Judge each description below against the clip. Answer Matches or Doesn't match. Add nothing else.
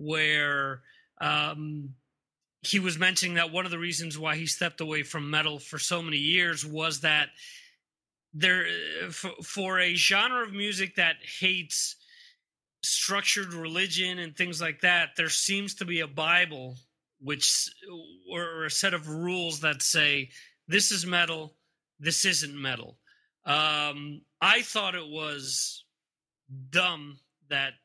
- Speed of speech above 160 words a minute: Doesn't match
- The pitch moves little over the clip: Doesn't match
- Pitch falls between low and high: Matches